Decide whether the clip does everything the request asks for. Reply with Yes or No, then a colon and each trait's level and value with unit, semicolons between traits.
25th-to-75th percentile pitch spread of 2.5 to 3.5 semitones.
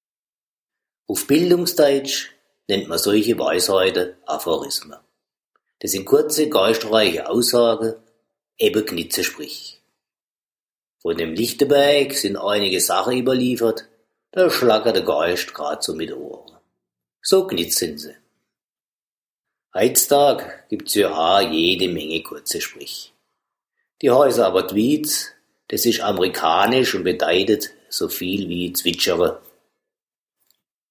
No: wide, 5.4 semitones